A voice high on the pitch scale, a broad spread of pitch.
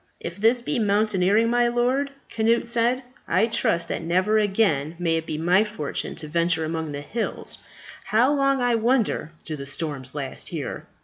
Yes: high, 205 Hz; wide, 6.5 semitones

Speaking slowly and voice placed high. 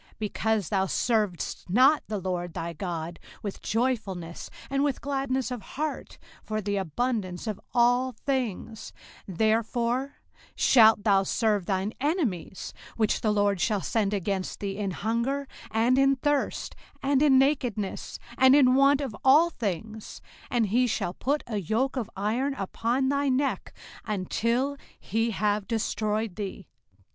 No: average, 145 wpm; high, 225 Hz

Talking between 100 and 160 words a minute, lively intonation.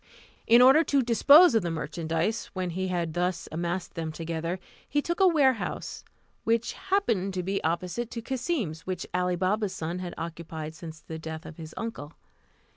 No: average, 175 wpm; wide, 5.9 semitones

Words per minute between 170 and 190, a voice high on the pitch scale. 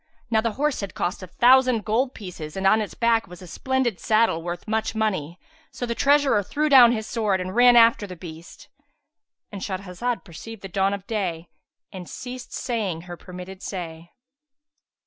Yes: average, 175 wpm; high, 210 Hz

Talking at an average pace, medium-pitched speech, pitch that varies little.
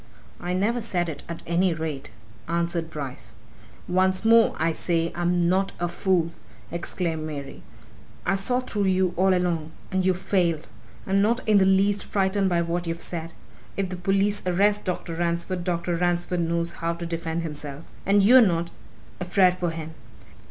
Yes: average, 165 wpm; medium, 175 Hz; narrow, 2.3 semitones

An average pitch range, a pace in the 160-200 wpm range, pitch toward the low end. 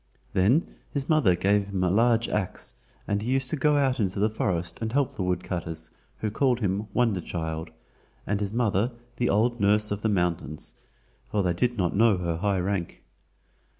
Yes: average, 4.6 semitones; average, 185 wpm; low, 100 Hz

